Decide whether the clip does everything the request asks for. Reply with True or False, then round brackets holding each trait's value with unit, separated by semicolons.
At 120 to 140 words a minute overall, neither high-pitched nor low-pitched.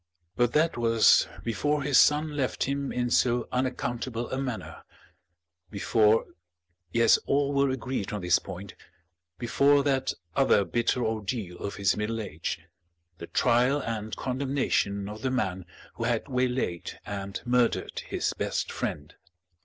False (135 wpm; 120 Hz)